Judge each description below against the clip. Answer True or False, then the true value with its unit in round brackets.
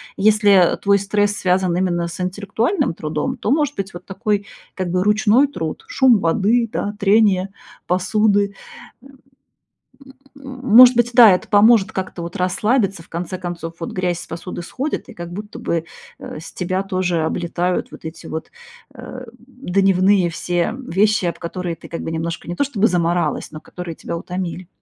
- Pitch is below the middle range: False (190 Hz)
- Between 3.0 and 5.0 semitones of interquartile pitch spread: True (3.6 semitones)